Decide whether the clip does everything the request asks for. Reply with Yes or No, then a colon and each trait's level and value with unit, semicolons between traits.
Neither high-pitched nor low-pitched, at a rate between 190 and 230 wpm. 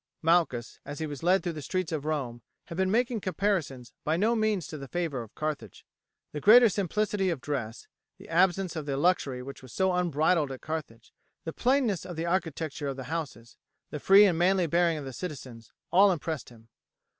Yes: medium, 165 Hz; average, 200 wpm